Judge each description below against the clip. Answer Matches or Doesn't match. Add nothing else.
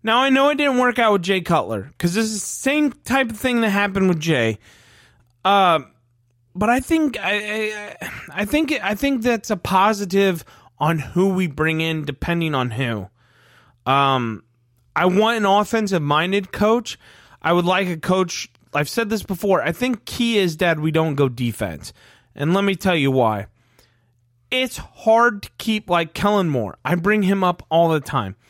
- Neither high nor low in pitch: Matches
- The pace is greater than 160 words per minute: Matches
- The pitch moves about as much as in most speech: Doesn't match